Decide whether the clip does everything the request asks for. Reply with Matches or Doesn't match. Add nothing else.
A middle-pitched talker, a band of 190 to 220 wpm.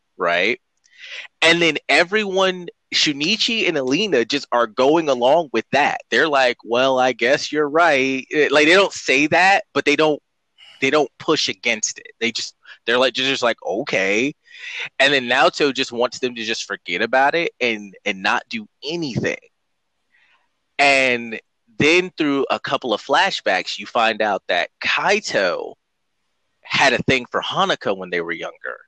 Doesn't match